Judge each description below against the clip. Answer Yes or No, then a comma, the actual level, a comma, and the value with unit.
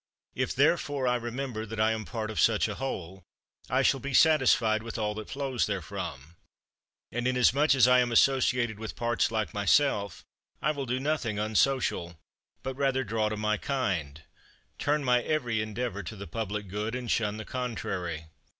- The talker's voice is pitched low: Yes, low, 115 Hz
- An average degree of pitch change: Yes, average, 3.7 semitones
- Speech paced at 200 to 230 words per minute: No, average, 175 wpm